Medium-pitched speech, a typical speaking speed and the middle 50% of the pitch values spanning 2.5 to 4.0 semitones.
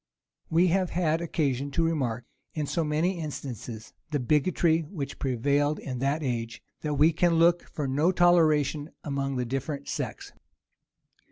Yes: medium, 150 Hz; average, 150 wpm; average, 3.3 semitones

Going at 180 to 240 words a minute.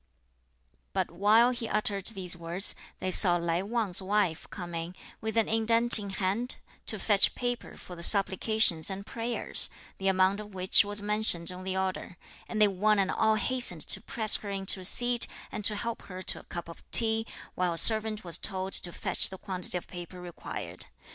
Yes: average, 190 wpm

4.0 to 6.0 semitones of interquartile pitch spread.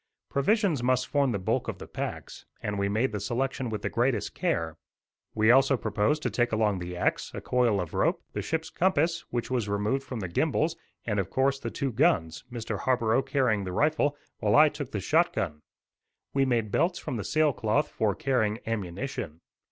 Yes: average, 4.9 semitones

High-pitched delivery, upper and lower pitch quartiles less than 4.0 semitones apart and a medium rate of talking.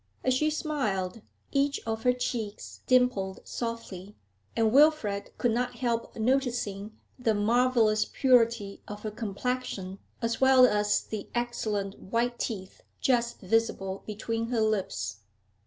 No: high, 230 Hz; average, 3.3 semitones; slow, 125 wpm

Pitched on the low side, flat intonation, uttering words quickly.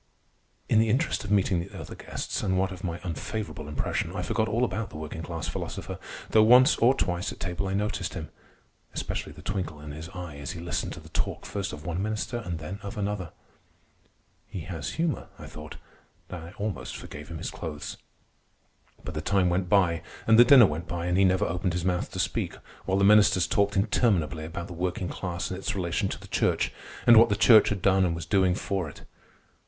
No: very low, 95 Hz; average, 3.3 semitones; fast, 215 wpm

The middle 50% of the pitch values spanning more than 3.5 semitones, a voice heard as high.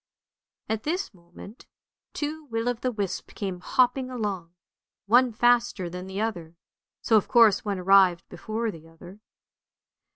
Yes: average, 4.8 semitones; high, 210 Hz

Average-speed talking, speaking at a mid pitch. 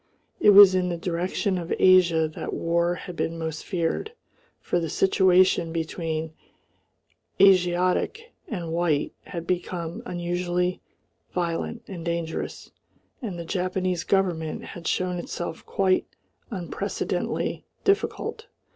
No: slow, 115 wpm; medium, 175 Hz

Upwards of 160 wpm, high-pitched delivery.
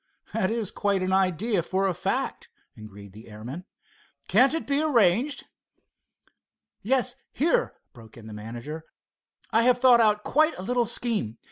No: average, 150 wpm; high, 200 Hz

